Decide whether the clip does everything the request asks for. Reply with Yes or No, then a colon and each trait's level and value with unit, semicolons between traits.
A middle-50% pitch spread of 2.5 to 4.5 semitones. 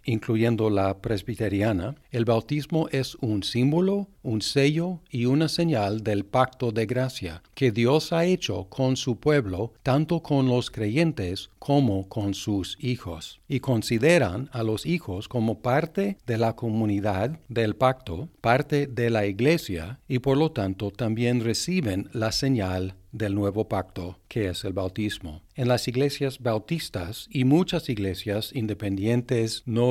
No: average, 4.9 semitones